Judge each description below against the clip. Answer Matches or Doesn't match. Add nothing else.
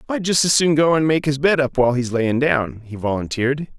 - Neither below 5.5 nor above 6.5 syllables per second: Matches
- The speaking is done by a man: Matches